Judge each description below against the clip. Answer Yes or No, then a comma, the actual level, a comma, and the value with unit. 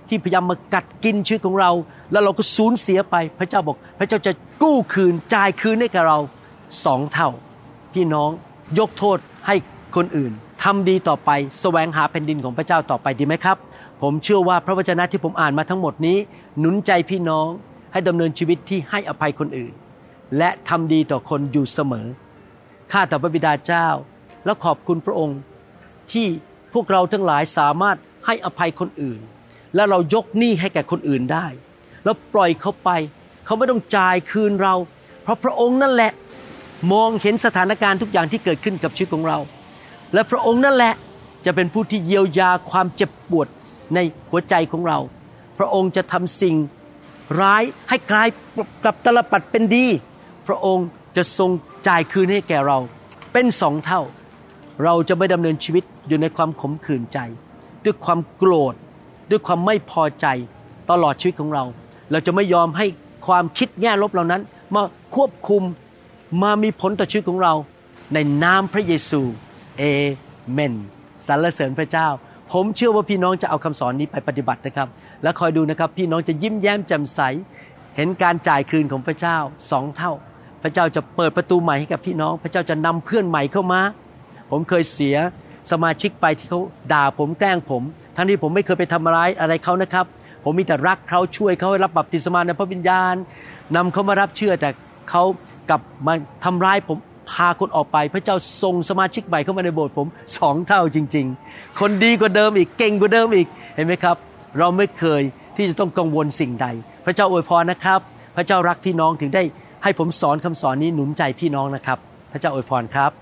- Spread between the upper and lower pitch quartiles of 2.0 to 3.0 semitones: No, average, 4.2 semitones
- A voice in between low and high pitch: Yes, medium, 175 Hz